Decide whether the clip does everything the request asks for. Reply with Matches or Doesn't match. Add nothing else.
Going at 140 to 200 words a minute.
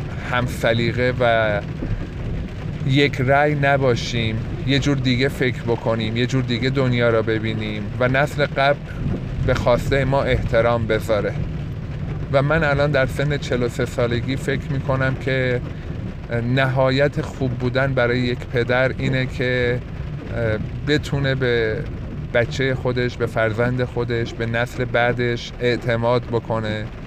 Doesn't match